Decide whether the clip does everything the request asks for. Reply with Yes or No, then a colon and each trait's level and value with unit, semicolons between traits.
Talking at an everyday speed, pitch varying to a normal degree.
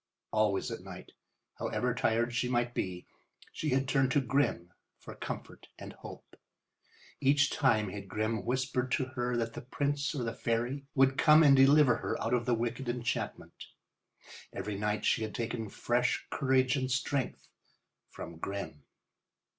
Yes: average, 155 wpm; average, 3.0 semitones